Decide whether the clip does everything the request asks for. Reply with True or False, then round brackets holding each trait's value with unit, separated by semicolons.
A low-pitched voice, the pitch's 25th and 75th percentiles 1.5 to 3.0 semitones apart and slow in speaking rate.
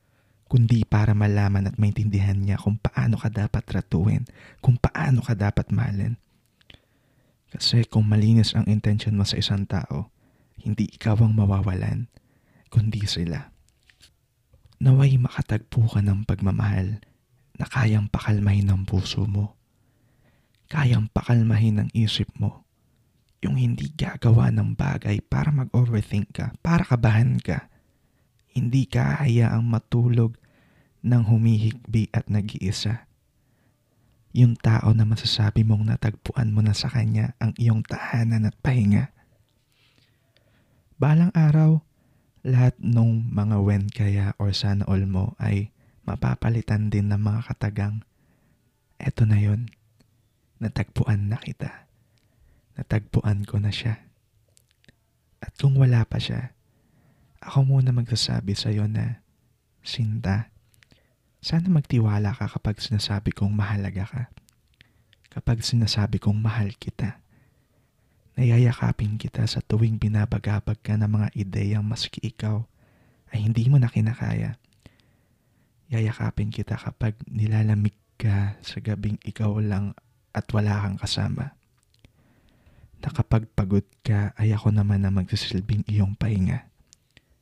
True (110 Hz; 2.6 semitones; 115 wpm)